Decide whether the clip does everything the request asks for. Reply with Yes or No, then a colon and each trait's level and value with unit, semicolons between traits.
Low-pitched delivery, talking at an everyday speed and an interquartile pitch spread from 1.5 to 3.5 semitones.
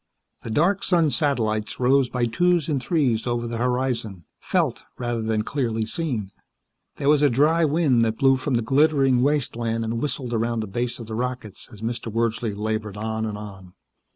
No: low, 120 Hz; average, 180 wpm; average, 3.9 semitones